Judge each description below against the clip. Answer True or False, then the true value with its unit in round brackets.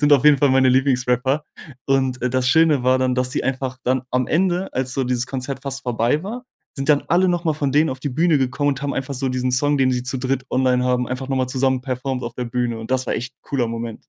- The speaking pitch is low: True (130 Hz)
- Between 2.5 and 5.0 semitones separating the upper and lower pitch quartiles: False (1.8 semitones)